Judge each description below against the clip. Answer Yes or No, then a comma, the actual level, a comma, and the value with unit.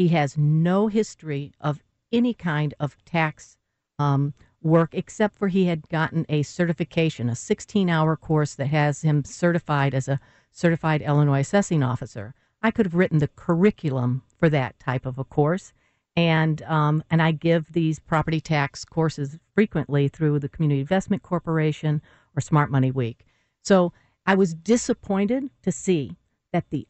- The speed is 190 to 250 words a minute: No, average, 155 wpm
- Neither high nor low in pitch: Yes, medium, 155 Hz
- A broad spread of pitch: No, average, 3.6 semitones